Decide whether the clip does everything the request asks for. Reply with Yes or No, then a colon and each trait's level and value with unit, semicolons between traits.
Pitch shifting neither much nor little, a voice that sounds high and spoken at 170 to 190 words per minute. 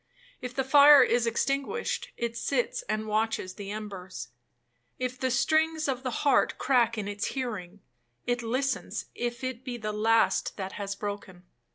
No: average, 3.9 semitones; high, 235 Hz; average, 160 wpm